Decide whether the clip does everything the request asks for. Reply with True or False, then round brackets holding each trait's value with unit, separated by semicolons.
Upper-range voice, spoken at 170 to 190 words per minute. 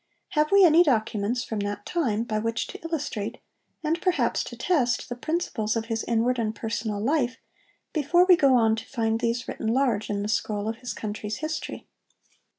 True (235 Hz; 185 wpm)